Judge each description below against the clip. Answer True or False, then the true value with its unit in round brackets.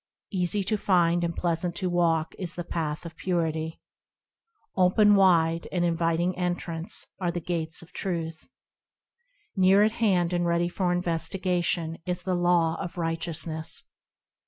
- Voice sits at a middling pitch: True (175 Hz)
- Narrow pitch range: True (1.6 semitones)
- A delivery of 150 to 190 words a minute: False (140 wpm)